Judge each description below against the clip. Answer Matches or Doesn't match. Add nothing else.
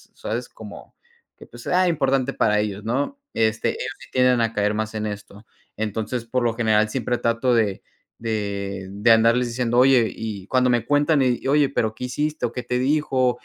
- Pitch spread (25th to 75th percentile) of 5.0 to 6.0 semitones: Doesn't match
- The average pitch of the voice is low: Matches